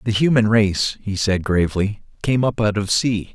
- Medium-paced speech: Yes, average, 195 wpm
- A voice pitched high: No, low, 105 Hz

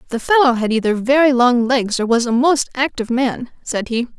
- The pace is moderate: No, fast, 215 wpm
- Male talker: No, female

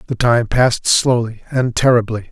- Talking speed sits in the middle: Yes, average, 155 wpm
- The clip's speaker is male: Yes, male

